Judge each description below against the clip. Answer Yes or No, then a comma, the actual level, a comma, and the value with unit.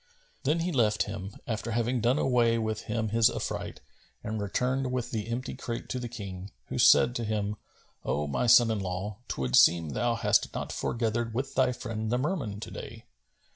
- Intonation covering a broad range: No, average, 2.9 semitones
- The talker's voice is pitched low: Yes, low, 115 Hz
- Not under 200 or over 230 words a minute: No, average, 190 wpm